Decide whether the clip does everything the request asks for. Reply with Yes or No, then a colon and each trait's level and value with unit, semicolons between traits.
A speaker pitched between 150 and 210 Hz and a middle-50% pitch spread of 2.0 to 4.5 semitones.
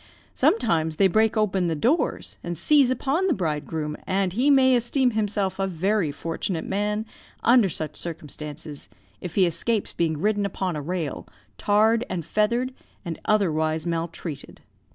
No: high, 190 Hz; average, 5.2 semitones